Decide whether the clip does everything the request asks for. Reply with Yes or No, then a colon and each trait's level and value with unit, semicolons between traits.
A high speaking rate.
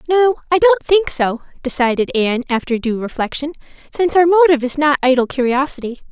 No: average, 165 wpm